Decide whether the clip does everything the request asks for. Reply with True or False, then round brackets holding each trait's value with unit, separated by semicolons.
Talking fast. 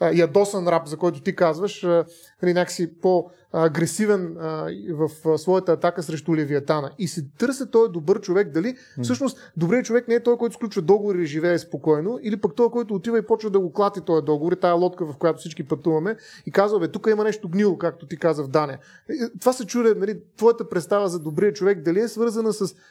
True (195 wpm)